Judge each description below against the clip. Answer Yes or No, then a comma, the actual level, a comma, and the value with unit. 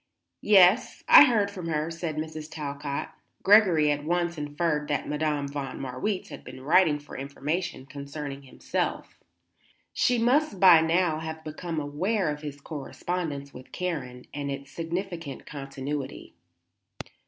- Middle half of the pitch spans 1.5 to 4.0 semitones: Yes, average, 3.7 semitones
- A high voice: No, medium, 155 Hz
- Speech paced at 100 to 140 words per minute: Yes, slow, 135 wpm